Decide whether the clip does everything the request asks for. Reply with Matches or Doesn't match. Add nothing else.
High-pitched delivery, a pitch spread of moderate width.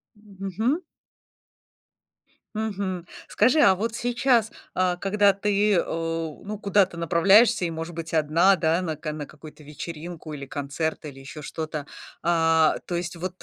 Doesn't match